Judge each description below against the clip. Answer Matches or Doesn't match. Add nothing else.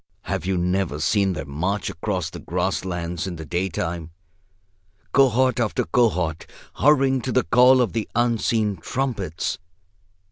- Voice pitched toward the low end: Matches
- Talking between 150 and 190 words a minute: Doesn't match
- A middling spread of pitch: Doesn't match